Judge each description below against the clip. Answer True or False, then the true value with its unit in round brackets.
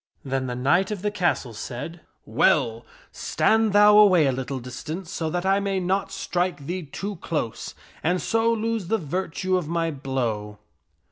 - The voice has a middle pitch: True (175 Hz)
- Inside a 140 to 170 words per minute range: False (180 wpm)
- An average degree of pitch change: False (6.5 semitones)